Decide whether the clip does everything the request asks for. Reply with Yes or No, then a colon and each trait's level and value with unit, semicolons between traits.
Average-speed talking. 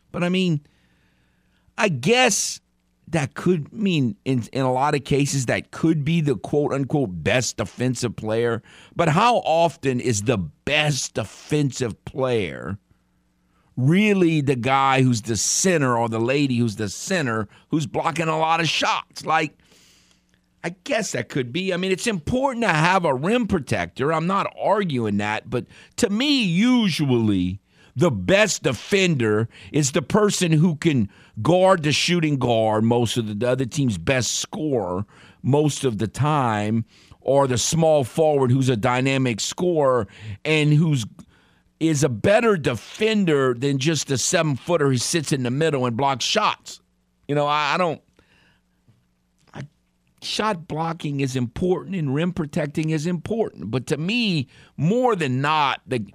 Yes: average, 155 wpm